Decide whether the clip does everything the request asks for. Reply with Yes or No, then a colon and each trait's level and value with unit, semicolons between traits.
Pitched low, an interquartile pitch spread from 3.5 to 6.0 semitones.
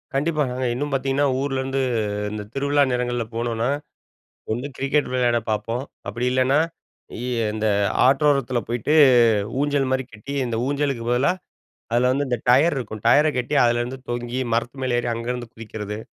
No: low, 125 Hz; narrow, 2.6 semitones